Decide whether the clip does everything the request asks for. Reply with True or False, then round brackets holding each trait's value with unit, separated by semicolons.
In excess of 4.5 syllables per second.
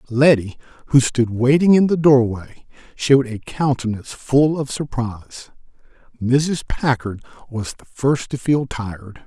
False (4.4 syllables/s)